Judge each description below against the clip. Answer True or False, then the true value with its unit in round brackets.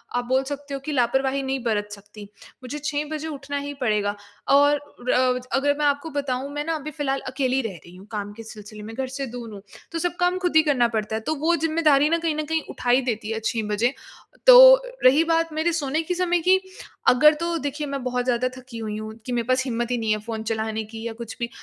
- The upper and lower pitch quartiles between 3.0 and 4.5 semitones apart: False (5.0 semitones)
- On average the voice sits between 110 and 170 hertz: False (265 Hz)